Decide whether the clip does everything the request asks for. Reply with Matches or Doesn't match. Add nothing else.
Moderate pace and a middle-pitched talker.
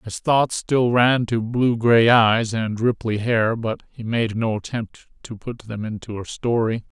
Doesn't match